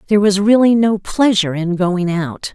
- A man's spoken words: No, female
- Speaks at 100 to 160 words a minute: No, average, 190 wpm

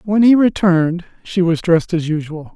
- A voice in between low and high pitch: Yes, medium, 175 Hz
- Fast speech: No, average, 190 wpm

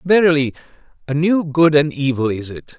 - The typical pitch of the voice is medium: Yes, medium, 150 Hz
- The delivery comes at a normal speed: Yes, average, 170 wpm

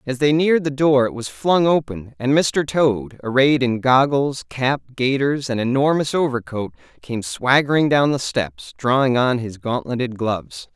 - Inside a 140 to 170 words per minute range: Yes, average, 165 wpm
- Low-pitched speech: Yes, low, 130 Hz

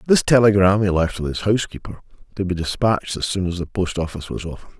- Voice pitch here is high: No, very low, 95 Hz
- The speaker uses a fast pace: Yes, fast, 215 wpm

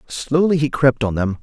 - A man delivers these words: Yes, male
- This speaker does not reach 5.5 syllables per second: Yes, 4.8 syllables/s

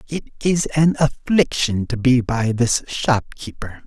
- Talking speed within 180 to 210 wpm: No, average, 140 wpm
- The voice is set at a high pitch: No, low, 130 Hz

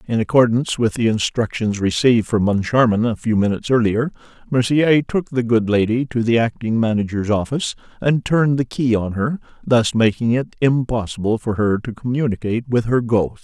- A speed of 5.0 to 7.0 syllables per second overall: Yes, 5.5 syllables/s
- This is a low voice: Yes, low, 115 Hz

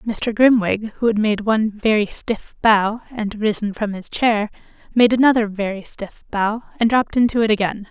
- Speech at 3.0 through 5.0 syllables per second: Yes, 4.9 syllables/s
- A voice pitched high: Yes, high, 215 Hz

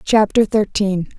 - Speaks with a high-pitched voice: Yes, high, 205 Hz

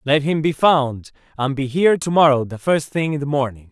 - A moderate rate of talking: No, fast, 240 wpm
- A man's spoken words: Yes, male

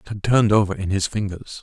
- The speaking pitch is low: Yes, low, 100 Hz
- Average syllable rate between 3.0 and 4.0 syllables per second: No, 6.5 syllables/s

